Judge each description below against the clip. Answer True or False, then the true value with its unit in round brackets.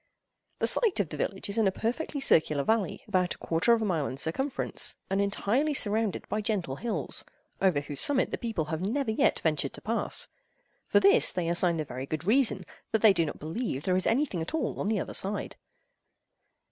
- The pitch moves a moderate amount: False (5.8 semitones)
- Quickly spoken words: True (210 wpm)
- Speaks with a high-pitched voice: True (200 Hz)